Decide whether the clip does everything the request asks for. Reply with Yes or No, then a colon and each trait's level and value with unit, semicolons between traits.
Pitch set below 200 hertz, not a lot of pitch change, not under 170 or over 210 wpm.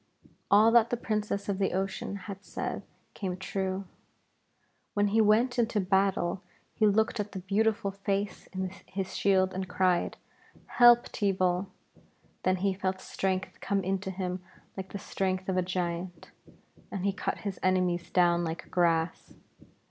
No: high, 190 Hz; narrow, 1.6 semitones; average, 150 wpm